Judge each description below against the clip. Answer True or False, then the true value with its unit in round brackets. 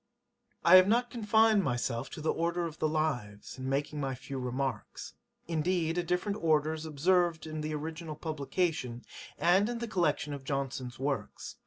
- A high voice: False (155 Hz)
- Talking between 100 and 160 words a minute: False (170 wpm)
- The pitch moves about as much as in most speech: True (4.3 semitones)